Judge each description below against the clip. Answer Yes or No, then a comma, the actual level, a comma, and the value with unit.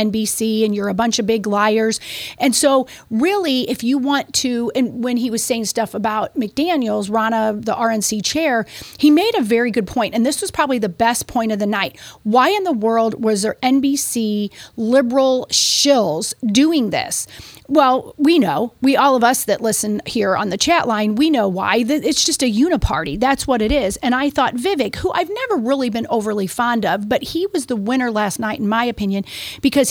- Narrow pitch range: No, average, 4.0 semitones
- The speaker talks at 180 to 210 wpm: Yes, fast, 205 wpm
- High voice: Yes, high, 240 Hz